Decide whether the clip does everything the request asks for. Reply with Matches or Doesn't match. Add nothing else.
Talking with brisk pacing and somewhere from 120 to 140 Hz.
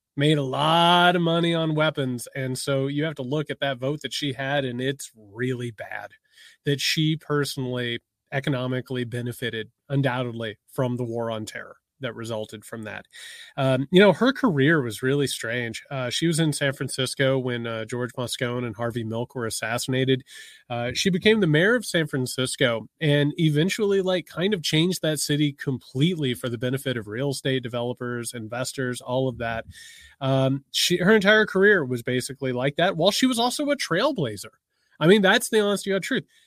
Doesn't match